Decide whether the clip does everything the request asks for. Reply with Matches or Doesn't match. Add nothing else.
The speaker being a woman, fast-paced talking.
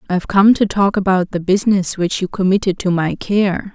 Matches